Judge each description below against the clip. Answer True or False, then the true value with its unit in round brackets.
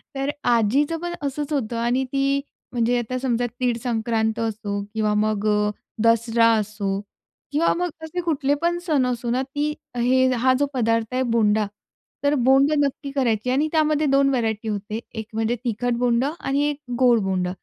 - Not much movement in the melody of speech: False (3.8 semitones)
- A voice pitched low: False (245 Hz)